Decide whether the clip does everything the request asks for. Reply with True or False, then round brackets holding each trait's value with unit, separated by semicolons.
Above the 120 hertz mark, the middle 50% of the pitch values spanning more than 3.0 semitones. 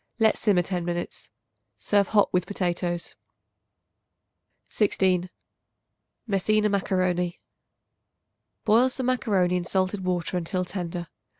False (185 Hz; 2.6 semitones)